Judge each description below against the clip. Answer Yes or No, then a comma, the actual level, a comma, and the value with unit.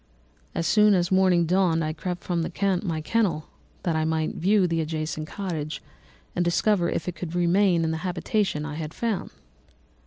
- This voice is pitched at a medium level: Yes, medium, 175 Hz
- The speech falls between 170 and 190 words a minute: Yes, average, 175 wpm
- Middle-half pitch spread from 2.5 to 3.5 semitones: Yes, average, 2.9 semitones